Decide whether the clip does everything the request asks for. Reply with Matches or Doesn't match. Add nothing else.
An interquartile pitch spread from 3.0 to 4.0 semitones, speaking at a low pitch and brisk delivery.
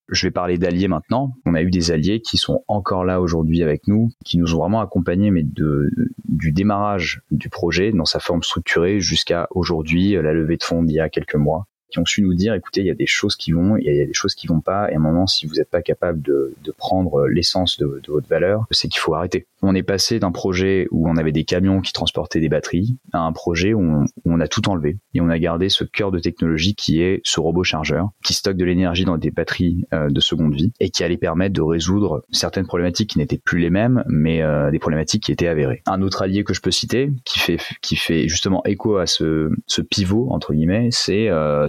Matches